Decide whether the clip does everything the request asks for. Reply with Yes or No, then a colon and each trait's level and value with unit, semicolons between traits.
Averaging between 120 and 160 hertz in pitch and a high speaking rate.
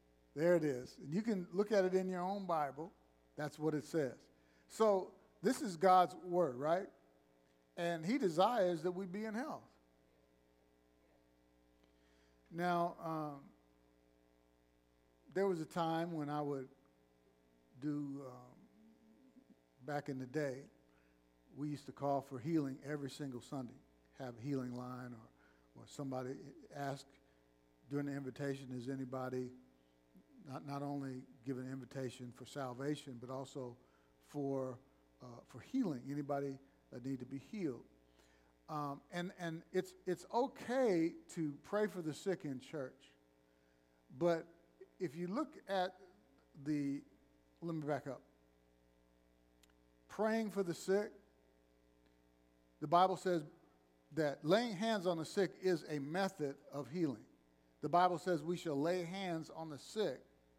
No: medium, 140 Hz; average, 140 wpm